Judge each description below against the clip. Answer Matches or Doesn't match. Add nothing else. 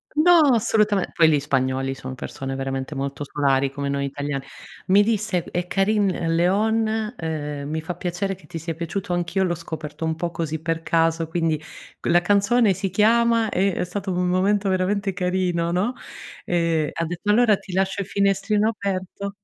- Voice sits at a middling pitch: Matches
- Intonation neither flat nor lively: Matches